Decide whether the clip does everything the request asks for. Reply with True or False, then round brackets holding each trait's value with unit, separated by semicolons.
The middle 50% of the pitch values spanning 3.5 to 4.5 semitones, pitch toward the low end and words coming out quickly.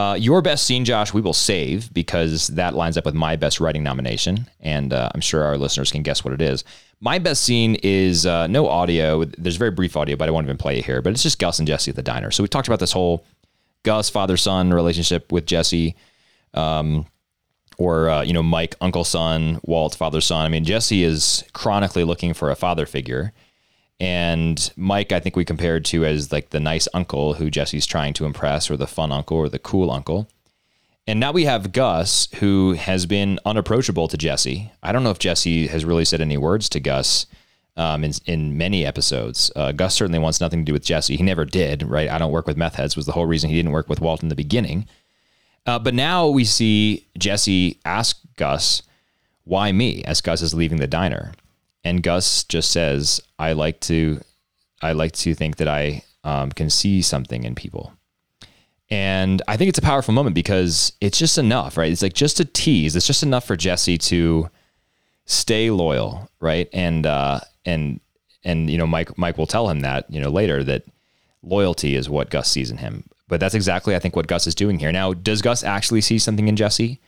True (4.1 semitones; 85 Hz; 210 wpm)